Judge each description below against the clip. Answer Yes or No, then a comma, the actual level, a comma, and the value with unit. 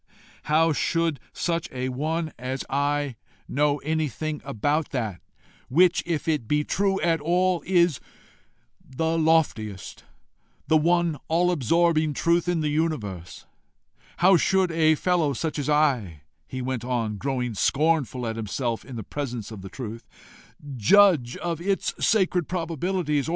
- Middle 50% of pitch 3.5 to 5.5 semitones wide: Yes, average, 4.8 semitones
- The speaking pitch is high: No, medium, 150 Hz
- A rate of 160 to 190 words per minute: No, average, 140 wpm